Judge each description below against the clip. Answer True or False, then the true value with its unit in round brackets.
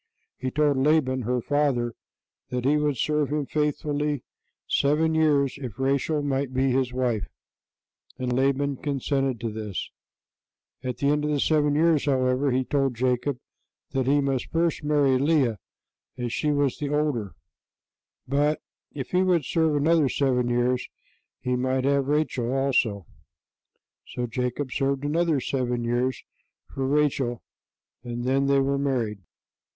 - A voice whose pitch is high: False (135 Hz)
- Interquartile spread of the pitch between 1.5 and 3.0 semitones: True (2.7 semitones)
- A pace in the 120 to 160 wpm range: True (145 wpm)